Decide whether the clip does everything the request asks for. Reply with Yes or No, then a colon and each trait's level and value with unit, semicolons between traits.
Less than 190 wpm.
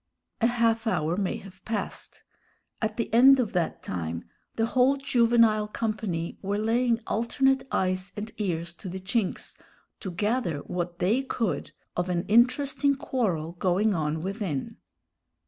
Yes: average, 145 wpm